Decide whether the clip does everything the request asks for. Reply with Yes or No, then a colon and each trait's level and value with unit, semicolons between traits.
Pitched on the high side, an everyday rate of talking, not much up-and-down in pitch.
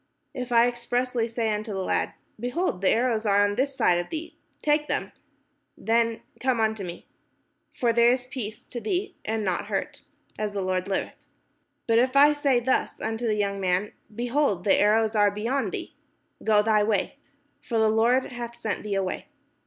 No: high, 225 Hz; average, 180 wpm; average, 3.2 semitones